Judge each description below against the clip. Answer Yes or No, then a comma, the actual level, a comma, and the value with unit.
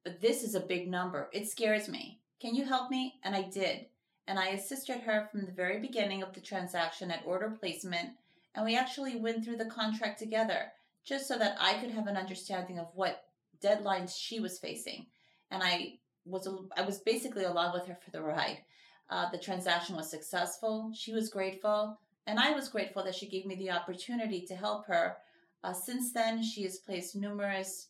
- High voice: Yes, high, 195 Hz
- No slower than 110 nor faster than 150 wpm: No, average, 200 wpm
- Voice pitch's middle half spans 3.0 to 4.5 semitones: Yes, average, 3.4 semitones